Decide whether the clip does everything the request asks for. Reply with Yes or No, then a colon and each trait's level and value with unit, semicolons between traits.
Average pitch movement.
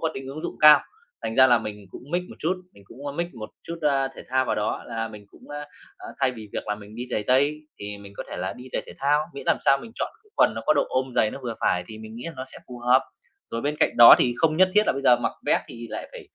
Yes: average, 4.6 semitones